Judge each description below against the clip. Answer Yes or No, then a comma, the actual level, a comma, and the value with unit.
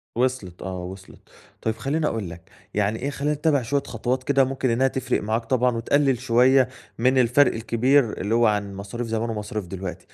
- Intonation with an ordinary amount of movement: Yes, average, 3.9 semitones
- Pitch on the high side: No, low, 120 Hz